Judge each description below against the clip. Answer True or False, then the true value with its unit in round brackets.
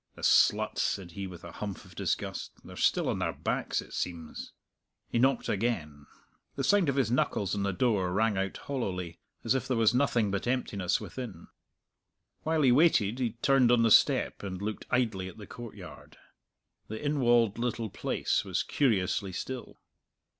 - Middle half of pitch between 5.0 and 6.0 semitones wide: False (4.5 semitones)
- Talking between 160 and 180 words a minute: True (175 wpm)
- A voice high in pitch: False (110 Hz)